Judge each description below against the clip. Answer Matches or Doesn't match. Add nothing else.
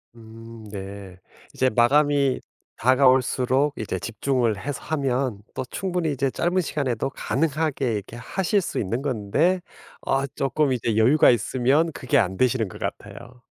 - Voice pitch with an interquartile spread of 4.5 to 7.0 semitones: Doesn't match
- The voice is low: Matches